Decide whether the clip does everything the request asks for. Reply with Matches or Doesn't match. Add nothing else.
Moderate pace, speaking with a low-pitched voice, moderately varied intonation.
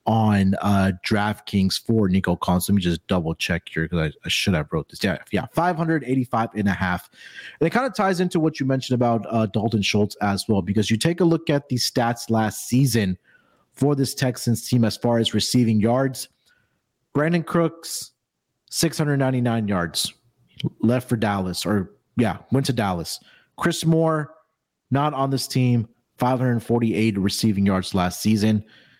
Matches